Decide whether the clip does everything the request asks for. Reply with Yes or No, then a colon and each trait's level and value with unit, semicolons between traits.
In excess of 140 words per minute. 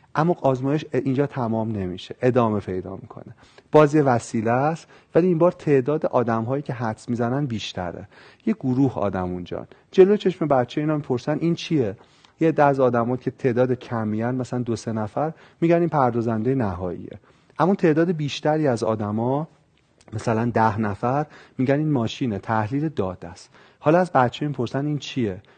Yes: fast, 155 wpm